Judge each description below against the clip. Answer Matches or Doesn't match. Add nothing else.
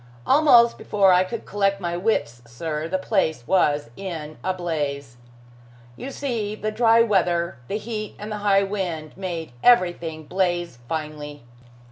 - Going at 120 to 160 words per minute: Matches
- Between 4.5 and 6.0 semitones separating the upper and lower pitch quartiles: Matches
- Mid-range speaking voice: Matches